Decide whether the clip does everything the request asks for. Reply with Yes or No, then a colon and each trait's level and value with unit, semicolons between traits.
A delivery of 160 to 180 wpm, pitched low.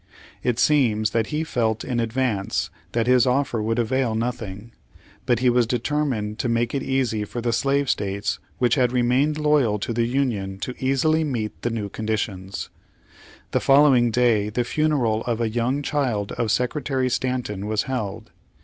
Yes: average, 165 wpm; low, 120 Hz